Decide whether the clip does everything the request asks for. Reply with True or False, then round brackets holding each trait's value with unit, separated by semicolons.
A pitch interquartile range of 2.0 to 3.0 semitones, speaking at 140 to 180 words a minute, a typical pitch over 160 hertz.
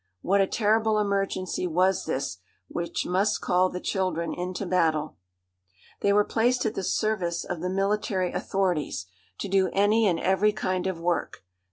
True (2.5 semitones; 160 wpm; 190 Hz)